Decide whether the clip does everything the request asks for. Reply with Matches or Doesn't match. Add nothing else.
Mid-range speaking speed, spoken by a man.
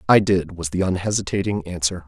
Matches